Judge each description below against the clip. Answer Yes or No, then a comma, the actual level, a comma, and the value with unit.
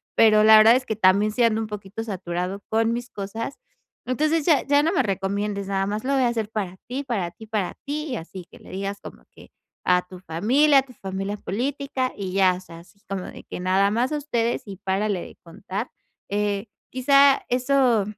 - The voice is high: Yes, high, 215 Hz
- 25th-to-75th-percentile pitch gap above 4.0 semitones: Yes, average, 4.6 semitones